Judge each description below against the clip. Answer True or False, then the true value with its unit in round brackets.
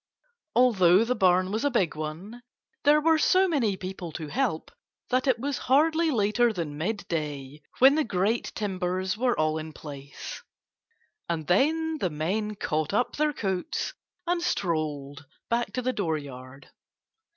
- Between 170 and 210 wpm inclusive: False (150 wpm)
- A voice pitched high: True (200 Hz)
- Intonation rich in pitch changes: True (8.2 semitones)